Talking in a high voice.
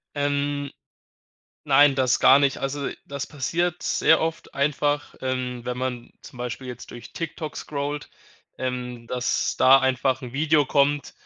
No: medium, 140 Hz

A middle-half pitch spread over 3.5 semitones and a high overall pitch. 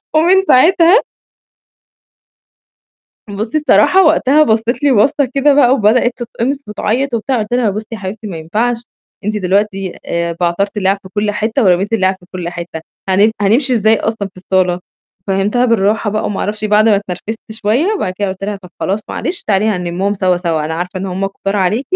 Yes: average, 4.0 semitones; high, 210 Hz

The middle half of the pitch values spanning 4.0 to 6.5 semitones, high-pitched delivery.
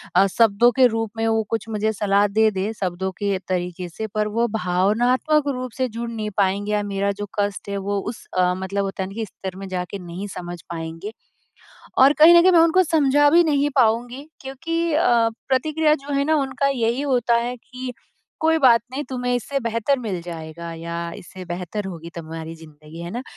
Yes: wide, 5.6 semitones; high, 220 Hz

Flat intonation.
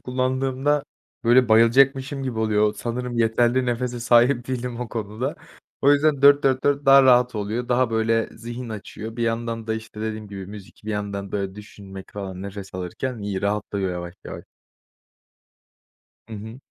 No: average, 3.5 semitones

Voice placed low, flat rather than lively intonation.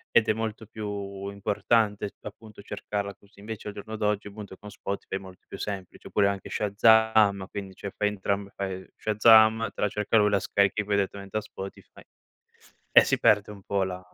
Yes: low, 100 Hz; narrow, 1.4 semitones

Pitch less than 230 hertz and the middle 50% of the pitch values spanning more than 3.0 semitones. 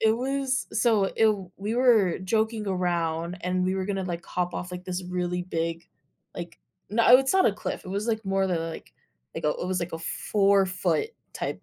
Yes: high, 190 Hz; average, 3.5 semitones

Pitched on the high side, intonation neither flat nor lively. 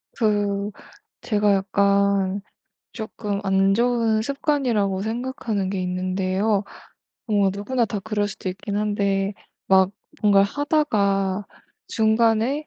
No: high, 205 Hz; narrow, 2.1 semitones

